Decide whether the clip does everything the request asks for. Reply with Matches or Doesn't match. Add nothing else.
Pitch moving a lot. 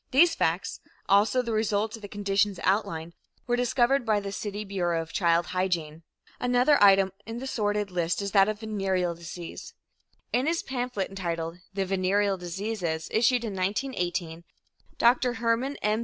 Doesn't match